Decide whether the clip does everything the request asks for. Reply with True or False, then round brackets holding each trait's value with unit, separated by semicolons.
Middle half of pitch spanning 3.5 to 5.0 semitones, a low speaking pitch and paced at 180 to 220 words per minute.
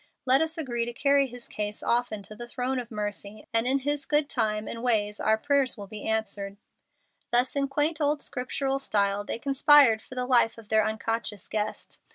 False (4.2 semitones; 240 Hz; 200 wpm)